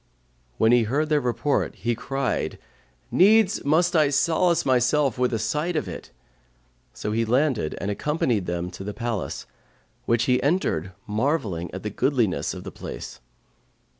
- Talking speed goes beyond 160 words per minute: No, average, 155 wpm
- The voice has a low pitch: Yes, low, 125 Hz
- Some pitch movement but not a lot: No, wide, 5.9 semitones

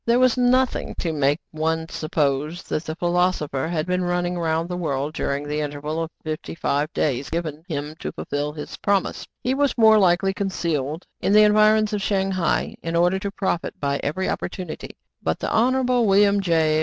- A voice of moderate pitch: Yes, medium, 170 Hz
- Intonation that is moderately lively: Yes, average, 4.5 semitones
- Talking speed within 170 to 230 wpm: Yes, average, 185 wpm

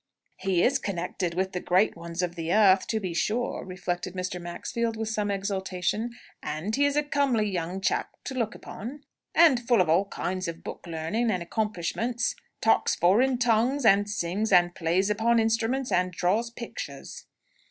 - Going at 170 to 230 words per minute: Yes, average, 175 wpm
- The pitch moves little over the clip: No, average, 4.6 semitones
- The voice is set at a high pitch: Yes, high, 200 Hz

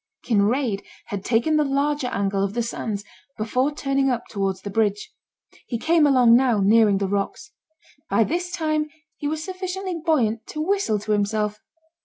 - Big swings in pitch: Yes, wide, 6.5 semitones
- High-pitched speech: Yes, high, 240 Hz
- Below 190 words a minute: Yes, average, 165 wpm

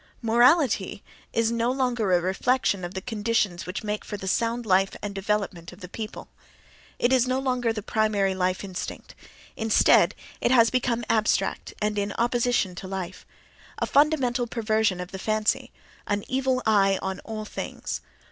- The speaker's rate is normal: Yes, average, 160 wpm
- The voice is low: No, high, 215 Hz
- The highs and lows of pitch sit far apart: No, average, 3.7 semitones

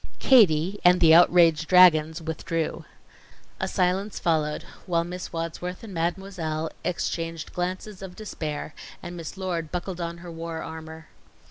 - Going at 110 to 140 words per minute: Yes, slow, 135 wpm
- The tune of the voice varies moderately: No, narrow, 2.1 semitones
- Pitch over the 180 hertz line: No, medium, 170 Hz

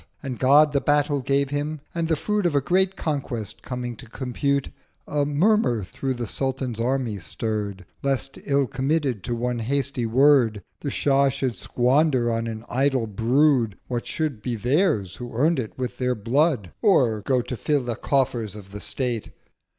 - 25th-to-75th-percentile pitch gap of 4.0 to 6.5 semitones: No, average, 3.5 semitones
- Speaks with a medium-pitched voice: No, low, 130 Hz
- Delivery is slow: No, average, 175 wpm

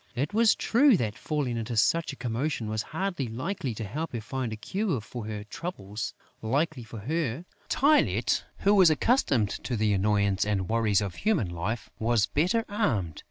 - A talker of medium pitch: No, low, 120 Hz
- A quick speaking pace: No, average, 175 wpm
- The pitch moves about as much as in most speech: No, wide, 7.6 semitones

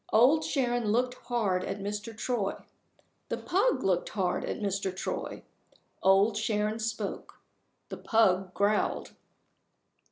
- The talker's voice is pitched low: No, high, 210 Hz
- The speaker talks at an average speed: No, slow, 120 wpm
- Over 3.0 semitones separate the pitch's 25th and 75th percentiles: Yes, average, 3.4 semitones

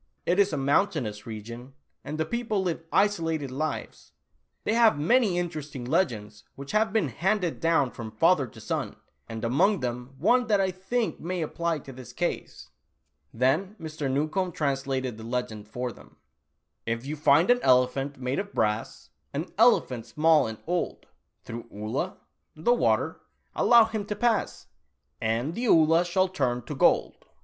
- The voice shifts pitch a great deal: Yes, wide, 7.0 semitones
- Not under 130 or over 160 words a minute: No, average, 170 wpm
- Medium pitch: Yes, medium, 155 Hz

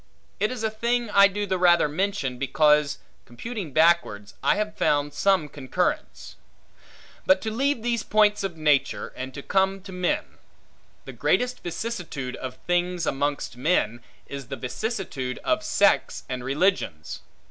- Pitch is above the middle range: No, medium, 175 Hz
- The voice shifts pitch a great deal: Yes, wide, 6.9 semitones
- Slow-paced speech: No, average, 145 wpm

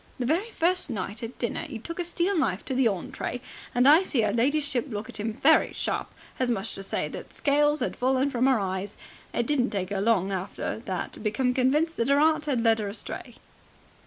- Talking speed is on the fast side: Yes, fast, 225 wpm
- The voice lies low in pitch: No, very high, 250 Hz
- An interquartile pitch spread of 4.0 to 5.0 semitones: No, wide, 5.6 semitones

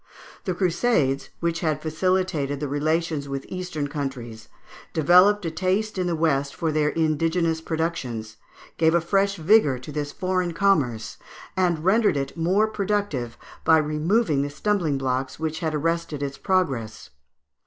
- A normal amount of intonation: Yes, average, 4.4 semitones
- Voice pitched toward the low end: No, medium, 160 Hz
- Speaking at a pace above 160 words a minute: No, average, 150 wpm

